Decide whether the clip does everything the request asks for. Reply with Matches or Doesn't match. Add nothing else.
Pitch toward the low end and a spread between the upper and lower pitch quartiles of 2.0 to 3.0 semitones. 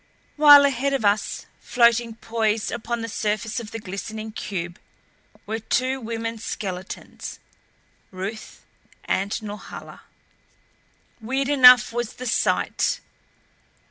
Doesn't match